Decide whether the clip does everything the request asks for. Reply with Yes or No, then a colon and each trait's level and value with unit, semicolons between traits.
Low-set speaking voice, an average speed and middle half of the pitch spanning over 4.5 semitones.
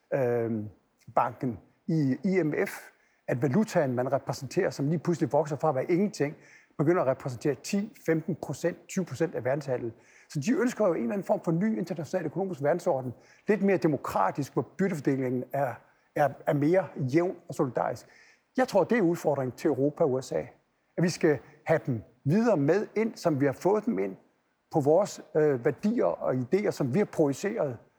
No: medium, 155 Hz; average, 170 wpm; wide, 5.4 semitones